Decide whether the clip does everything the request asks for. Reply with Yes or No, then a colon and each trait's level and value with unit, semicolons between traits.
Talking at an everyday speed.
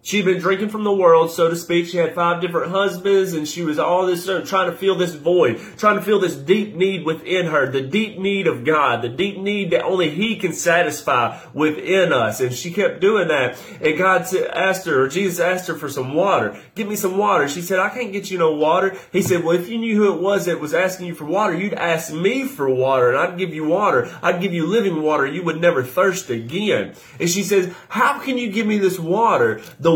No: fast, 240 wpm